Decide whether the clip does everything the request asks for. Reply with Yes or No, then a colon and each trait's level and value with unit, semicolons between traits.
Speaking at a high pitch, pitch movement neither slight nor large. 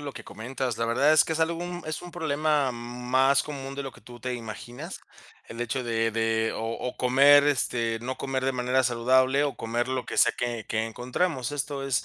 No: low, 130 Hz; average, 3.0 semitones